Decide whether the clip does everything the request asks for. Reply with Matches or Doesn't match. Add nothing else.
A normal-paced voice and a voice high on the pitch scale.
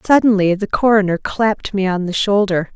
Matches